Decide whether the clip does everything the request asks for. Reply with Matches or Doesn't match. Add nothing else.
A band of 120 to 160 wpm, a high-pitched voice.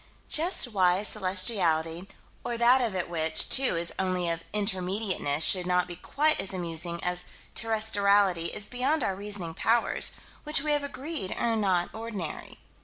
Matches